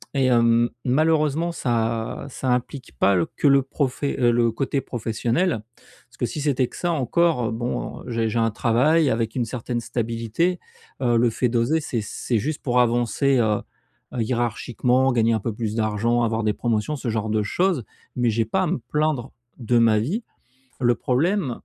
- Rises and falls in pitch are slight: No, average, 3.3 semitones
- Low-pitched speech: Yes, low, 120 Hz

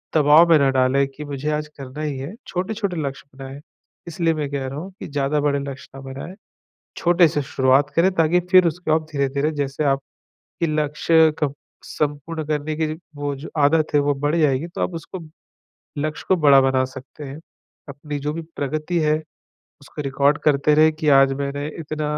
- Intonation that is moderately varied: No, narrow, 2.2 semitones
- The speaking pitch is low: No, medium, 150 Hz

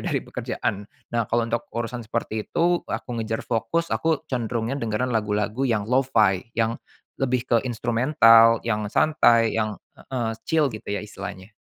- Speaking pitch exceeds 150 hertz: No, low, 115 Hz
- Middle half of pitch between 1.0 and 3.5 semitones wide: Yes, narrow, 2.5 semitones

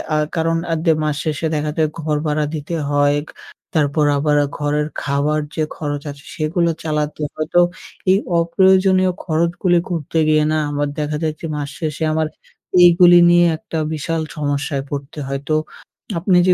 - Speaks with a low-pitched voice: No, medium, 155 Hz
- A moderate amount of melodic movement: No, narrow, 2.3 semitones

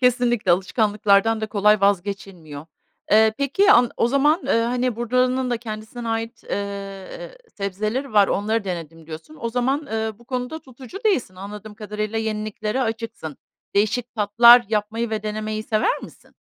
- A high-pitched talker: Yes, high, 220 Hz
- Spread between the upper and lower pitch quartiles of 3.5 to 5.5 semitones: No, average, 3.1 semitones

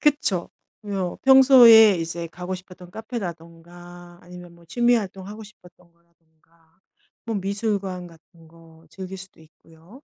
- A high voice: No, medium, 180 Hz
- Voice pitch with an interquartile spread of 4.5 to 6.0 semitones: No, average, 3.3 semitones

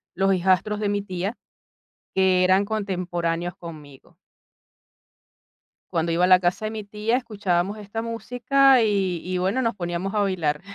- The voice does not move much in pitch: No, average, 3.2 semitones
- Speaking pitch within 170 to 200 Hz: Yes, high, 190 Hz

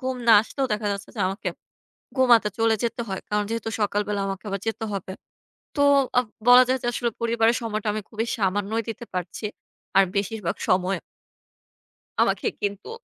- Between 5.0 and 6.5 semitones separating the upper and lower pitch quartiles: No, average, 2.7 semitones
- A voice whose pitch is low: No, high, 215 Hz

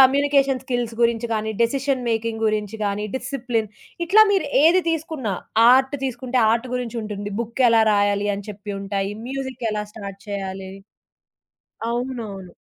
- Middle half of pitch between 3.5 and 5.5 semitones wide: Yes, average, 4.1 semitones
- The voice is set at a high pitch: Yes, high, 230 Hz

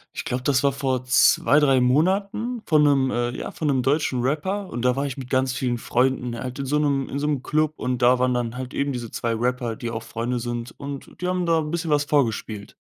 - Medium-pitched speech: No, low, 130 Hz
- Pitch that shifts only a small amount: No, average, 3.2 semitones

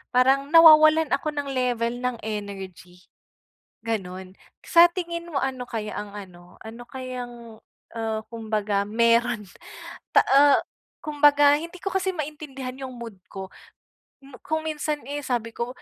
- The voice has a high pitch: Yes, very high, 250 Hz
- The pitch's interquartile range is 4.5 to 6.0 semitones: Yes, average, 5.0 semitones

